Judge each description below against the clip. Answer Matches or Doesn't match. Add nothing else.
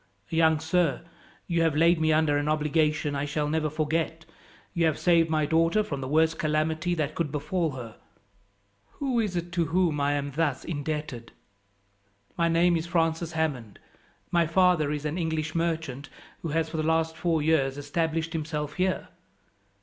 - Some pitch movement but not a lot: Doesn't match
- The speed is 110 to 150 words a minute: Doesn't match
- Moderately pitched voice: Matches